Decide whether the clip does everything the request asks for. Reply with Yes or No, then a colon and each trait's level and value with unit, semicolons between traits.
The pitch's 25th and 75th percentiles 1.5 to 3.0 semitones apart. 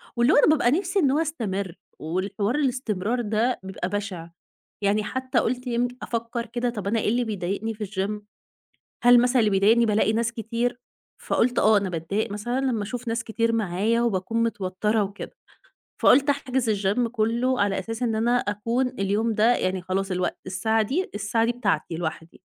No: average, 3.4 semitones